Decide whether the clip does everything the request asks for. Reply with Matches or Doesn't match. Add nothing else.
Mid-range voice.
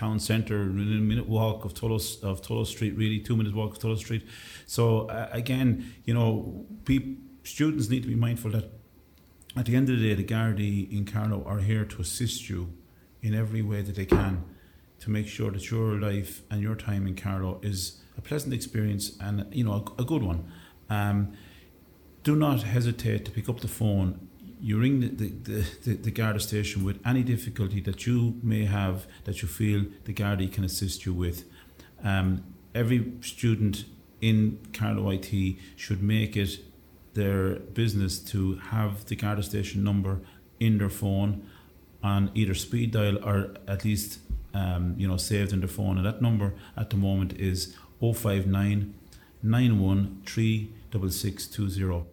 Doesn't match